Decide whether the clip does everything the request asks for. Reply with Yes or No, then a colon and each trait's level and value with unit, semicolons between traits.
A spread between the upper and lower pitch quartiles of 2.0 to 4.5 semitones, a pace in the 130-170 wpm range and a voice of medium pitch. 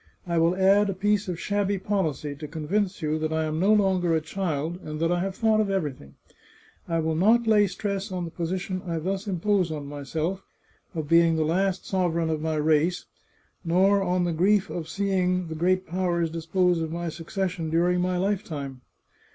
No: average, 3.2 semitones; average, 195 wpm; medium, 175 Hz